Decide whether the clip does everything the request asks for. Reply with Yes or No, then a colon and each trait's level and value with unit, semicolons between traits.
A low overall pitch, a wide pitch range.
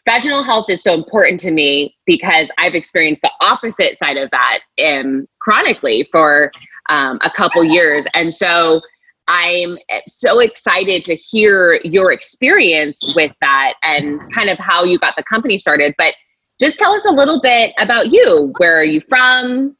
No: medium, 180 Hz; wide, 7.9 semitones